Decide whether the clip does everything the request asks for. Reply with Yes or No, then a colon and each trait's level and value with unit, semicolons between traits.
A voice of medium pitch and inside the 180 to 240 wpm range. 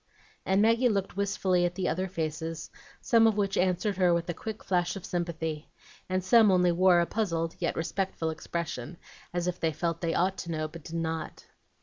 Yes: medium, 175 Hz; average, 200 wpm